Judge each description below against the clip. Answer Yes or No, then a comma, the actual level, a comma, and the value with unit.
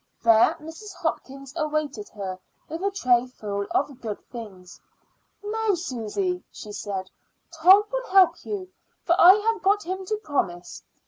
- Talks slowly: No, average, 145 wpm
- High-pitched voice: Yes, very high, 310 Hz